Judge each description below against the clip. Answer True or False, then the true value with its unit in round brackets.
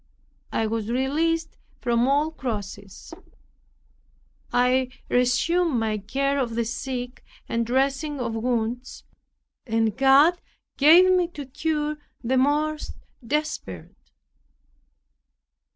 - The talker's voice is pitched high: True (260 Hz)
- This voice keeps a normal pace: False (100 wpm)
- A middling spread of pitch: True (4.3 semitones)